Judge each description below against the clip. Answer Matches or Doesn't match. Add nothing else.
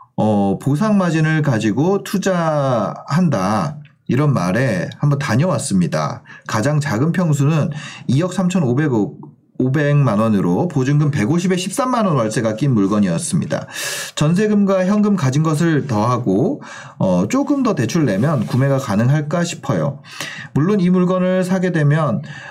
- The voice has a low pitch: Doesn't match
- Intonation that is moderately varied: Matches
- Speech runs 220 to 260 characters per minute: Matches